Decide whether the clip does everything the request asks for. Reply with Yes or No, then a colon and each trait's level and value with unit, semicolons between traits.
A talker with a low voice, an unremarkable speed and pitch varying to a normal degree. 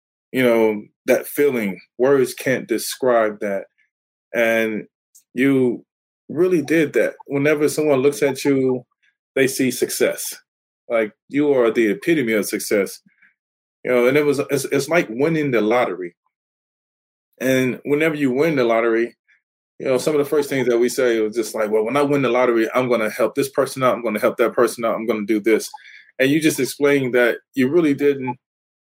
Yes: low, 130 Hz; average, 190 wpm; average, 4.2 semitones